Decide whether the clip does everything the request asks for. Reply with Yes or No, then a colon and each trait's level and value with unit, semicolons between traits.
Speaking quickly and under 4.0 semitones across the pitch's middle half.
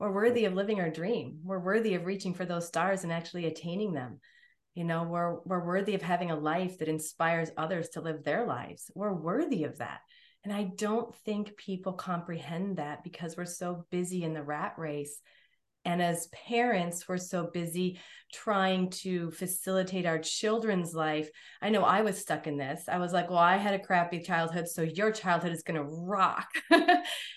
No: average, 190 wpm; average, 2.9 semitones